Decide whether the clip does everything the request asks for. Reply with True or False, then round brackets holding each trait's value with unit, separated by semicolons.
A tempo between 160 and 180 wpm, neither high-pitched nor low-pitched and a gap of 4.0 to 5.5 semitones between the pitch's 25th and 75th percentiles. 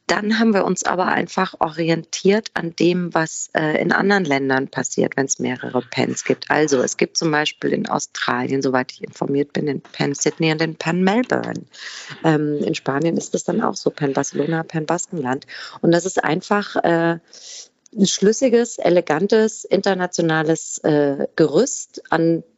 True (165 wpm; 165 Hz; 4.4 semitones)